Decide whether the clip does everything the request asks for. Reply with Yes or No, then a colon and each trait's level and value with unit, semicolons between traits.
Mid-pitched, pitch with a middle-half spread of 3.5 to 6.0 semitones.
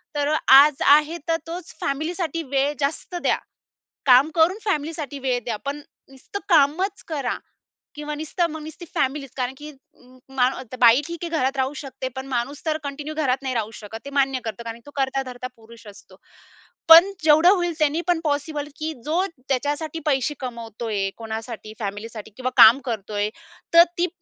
No: very high, 280 Hz; average, 4.0 semitones